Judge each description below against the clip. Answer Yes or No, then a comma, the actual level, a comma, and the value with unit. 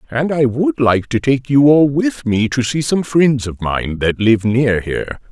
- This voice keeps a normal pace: No, fast, 225 wpm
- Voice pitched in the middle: No, low, 130 Hz